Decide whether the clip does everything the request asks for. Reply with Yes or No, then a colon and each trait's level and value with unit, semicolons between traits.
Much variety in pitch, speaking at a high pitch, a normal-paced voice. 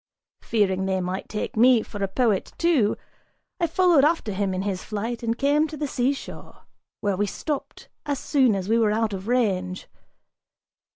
Yes: wide, 5.9 semitones; high, 225 Hz; average, 175 wpm